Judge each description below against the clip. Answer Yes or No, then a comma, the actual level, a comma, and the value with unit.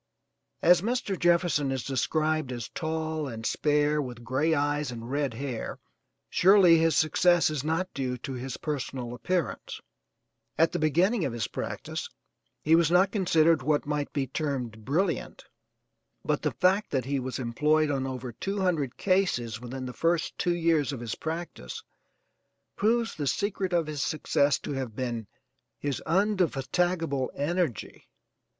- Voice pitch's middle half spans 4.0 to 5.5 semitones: Yes, average, 4.8 semitones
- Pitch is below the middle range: No, medium, 150 Hz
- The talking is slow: No, average, 150 wpm